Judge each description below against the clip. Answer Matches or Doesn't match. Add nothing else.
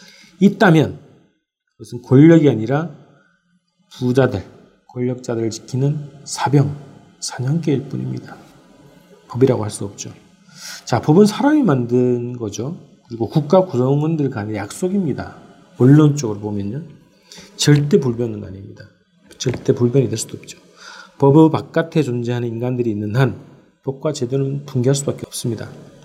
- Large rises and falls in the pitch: Doesn't match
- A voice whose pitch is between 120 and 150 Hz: Matches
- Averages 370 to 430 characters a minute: Doesn't match